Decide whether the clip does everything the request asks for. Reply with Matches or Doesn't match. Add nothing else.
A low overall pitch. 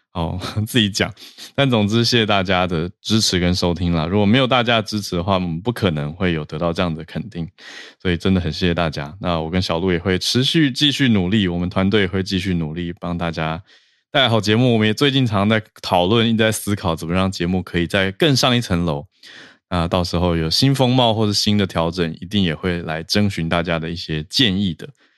Matches